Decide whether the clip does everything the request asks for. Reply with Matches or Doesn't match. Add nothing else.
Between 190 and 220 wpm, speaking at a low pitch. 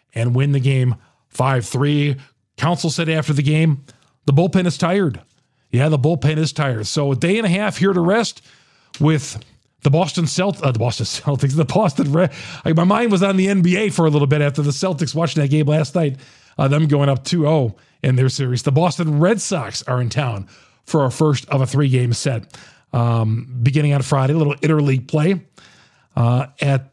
Doesn't match